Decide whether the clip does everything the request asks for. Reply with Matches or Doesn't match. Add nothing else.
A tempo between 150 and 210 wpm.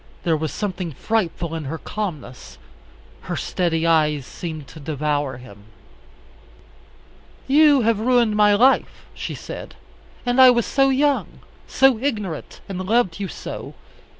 Doesn't match